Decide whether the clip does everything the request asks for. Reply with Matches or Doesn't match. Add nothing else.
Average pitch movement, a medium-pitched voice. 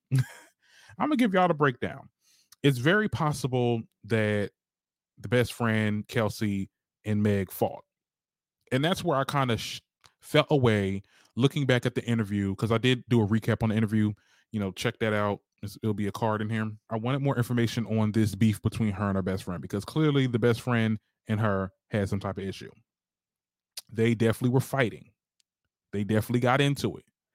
Doesn't match